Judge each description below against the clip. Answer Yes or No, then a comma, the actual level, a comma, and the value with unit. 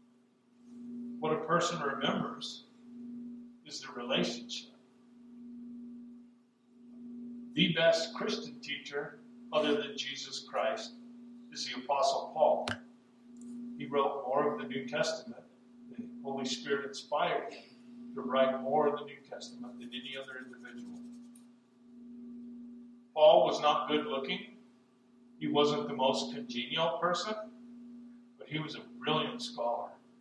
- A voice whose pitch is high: Yes, high, 240 Hz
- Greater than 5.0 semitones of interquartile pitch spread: Yes, wide, 5.4 semitones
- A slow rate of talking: Yes, slow, 115 wpm